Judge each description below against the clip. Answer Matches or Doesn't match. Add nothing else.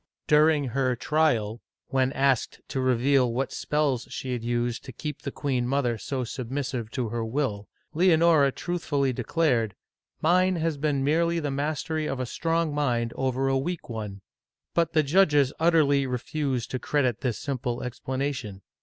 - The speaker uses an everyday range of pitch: Matches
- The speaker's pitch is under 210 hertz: Matches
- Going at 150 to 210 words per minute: Matches